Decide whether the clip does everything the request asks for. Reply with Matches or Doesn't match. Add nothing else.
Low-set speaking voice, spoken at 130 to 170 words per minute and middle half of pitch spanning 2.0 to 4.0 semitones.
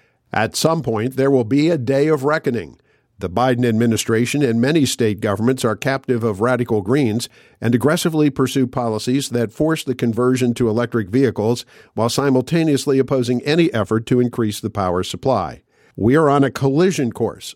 Matches